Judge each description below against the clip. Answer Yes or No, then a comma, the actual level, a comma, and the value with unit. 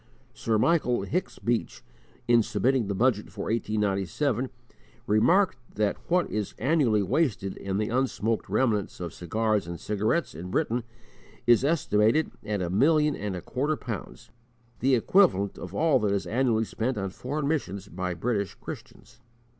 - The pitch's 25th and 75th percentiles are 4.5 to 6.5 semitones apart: Yes, average, 4.8 semitones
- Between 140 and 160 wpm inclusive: Yes, average, 150 wpm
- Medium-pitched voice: No, low, 110 Hz